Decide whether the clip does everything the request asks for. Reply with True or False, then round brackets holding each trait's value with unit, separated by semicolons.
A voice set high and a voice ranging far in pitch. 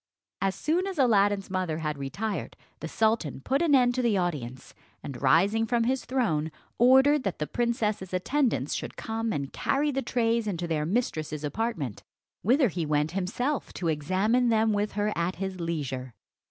True (205 Hz; 6.9 semitones)